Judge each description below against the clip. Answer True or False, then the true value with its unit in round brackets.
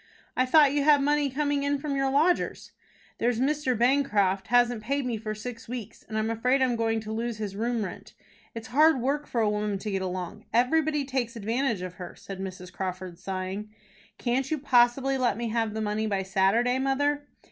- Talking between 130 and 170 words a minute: False (200 wpm)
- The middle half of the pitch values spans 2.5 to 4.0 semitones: False (4.4 semitones)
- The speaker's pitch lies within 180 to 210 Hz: False (240 Hz)